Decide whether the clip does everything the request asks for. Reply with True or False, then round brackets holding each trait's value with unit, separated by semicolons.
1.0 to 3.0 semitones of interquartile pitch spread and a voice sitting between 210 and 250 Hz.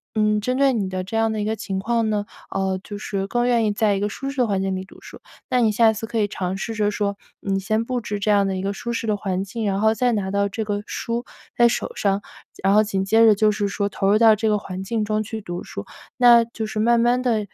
True (2.4 semitones; 215 Hz)